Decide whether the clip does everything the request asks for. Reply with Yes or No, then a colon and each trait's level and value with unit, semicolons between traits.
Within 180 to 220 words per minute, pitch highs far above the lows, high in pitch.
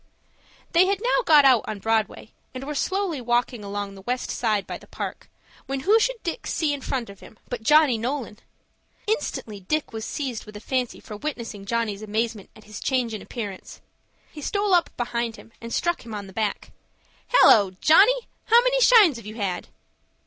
Yes: average, 190 wpm; wide, 6.3 semitones; high, 240 Hz